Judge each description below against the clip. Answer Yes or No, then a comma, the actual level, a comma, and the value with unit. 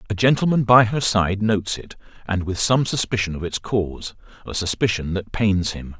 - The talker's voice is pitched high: No, low, 100 Hz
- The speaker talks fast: No, average, 180 wpm